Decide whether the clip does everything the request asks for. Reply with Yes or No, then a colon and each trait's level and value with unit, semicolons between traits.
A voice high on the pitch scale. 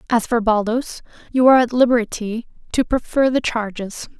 Yes: high, 230 Hz